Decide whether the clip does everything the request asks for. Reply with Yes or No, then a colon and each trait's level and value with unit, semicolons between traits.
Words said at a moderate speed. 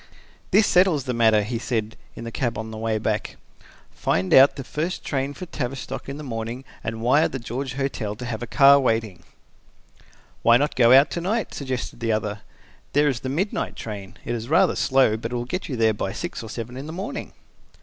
No: fast, 210 wpm